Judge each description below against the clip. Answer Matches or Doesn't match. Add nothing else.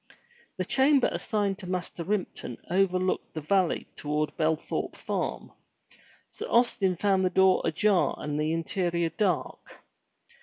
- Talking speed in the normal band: Doesn't match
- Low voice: Doesn't match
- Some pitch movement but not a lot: Matches